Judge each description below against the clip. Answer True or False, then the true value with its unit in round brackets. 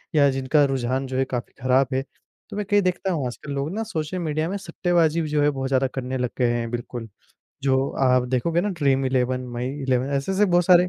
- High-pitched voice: False (135 Hz)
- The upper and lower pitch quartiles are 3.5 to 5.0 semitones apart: True (4.7 semitones)